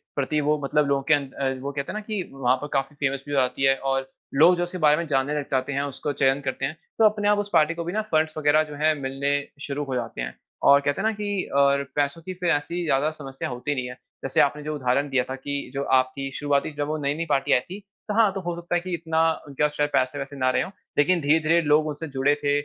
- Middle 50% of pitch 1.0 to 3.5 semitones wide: Yes, average, 2.9 semitones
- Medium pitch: Yes, medium, 145 Hz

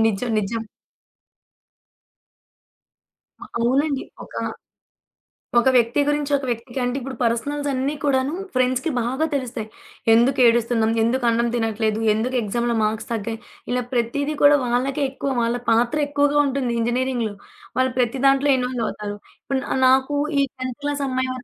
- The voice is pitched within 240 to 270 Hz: Yes, very high, 250 Hz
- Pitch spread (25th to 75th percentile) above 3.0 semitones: No, average, 2.7 semitones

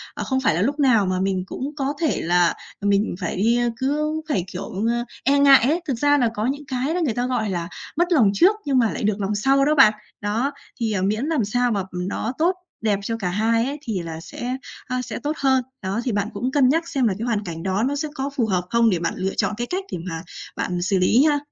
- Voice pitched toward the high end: Yes, high, 235 Hz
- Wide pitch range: Yes, wide, 5.7 semitones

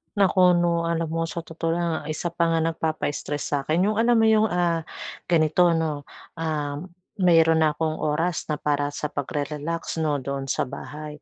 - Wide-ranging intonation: No, narrow, 2.4 semitones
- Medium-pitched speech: Yes, medium, 165 Hz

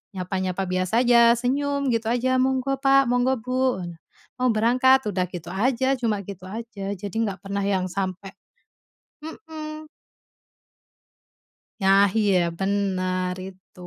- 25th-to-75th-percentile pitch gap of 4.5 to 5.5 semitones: Yes, average, 5.1 semitones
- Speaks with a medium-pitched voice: No, high, 220 Hz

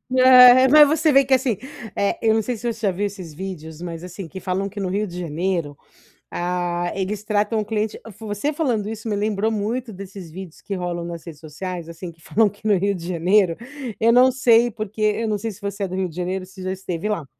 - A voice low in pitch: No, high, 200 Hz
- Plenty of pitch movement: No, average, 3.7 semitones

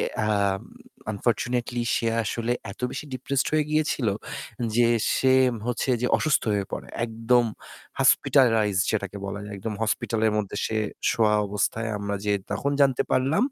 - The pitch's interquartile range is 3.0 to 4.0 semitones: Yes, average, 3.5 semitones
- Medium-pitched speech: No, low, 115 Hz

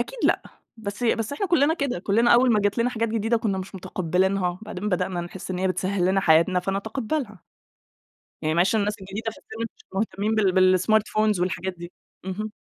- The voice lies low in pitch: No, high, 200 Hz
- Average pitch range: Yes, average, 3.2 semitones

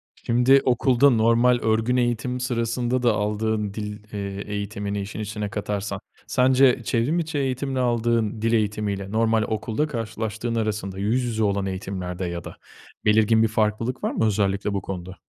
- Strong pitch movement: No, average, 2.8 semitones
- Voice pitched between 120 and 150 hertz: No, low, 110 Hz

